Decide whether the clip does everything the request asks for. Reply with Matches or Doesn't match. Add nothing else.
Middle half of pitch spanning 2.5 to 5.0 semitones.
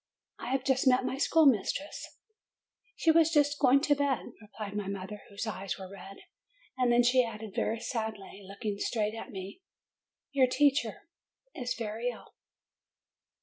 Matches